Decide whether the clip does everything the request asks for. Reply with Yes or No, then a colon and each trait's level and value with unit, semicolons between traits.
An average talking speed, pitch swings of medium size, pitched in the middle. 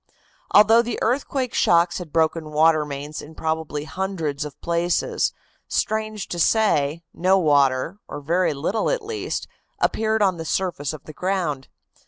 Yes: average, 150 wpm; average, 5.0 semitones; medium, 170 Hz